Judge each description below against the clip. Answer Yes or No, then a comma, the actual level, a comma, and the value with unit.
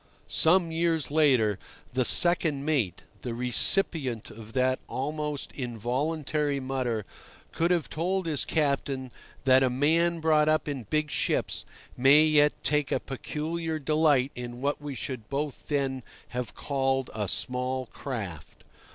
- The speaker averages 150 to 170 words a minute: No, slow, 135 wpm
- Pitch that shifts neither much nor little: Yes, average, 3.4 semitones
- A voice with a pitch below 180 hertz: Yes, medium, 140 Hz